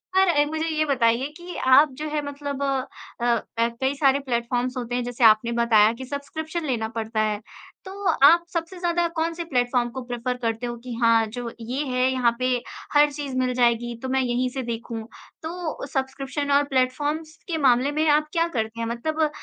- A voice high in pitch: Yes, very high, 260 Hz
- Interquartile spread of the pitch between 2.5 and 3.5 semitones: No, average, 4.0 semitones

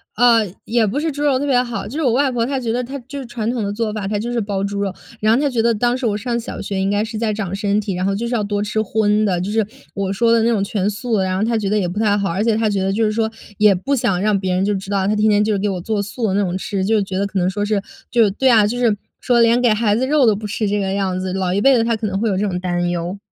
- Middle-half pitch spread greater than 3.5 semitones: No, average, 2.9 semitones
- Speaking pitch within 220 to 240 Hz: No, high, 210 Hz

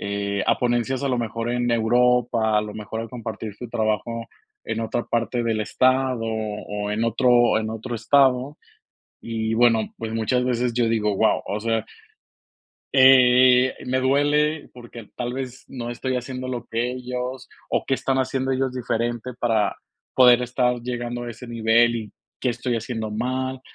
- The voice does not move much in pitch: Yes, narrow, 2.1 semitones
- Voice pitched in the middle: No, low, 120 Hz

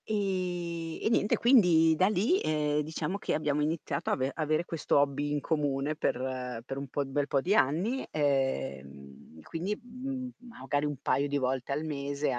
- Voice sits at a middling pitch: Yes, medium, 150 Hz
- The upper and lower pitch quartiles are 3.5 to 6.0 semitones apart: Yes, average, 4.3 semitones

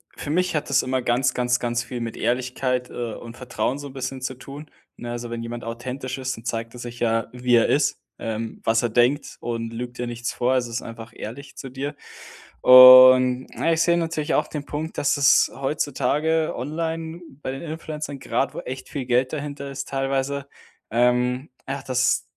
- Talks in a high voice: No, low, 130 Hz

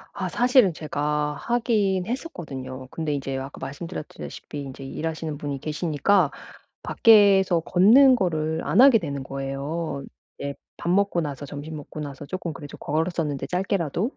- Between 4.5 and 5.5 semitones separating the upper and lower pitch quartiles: Yes, average, 5.1 semitones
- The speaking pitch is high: No, medium, 160 Hz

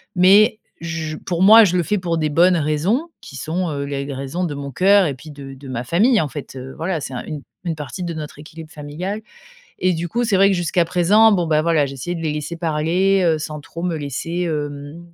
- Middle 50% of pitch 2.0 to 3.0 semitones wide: No, average, 3.6 semitones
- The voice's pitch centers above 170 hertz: No, medium, 165 Hz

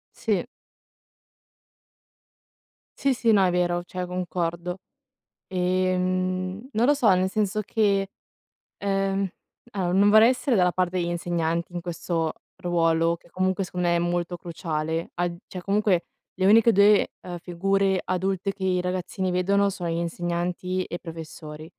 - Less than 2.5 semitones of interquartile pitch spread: Yes, narrow, 2.1 semitones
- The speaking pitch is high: No, medium, 180 Hz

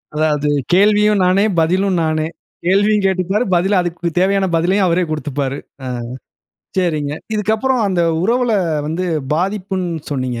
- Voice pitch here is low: No, medium, 185 Hz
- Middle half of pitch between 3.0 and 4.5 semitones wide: Yes, average, 4.1 semitones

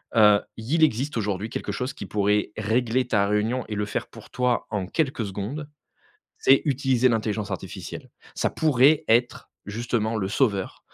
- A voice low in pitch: Yes, low, 115 Hz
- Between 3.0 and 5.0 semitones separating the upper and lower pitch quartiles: Yes, average, 3.7 semitones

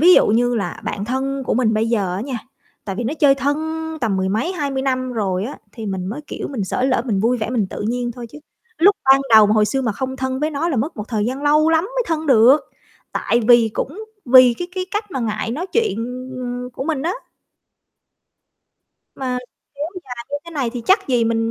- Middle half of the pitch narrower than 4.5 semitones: Yes, average, 4.1 semitones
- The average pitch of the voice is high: Yes, very high, 255 Hz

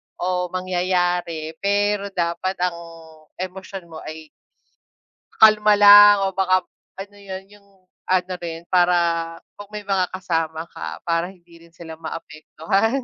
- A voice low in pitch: No, medium, 185 Hz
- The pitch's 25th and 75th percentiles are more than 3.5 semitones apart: No, average, 2.8 semitones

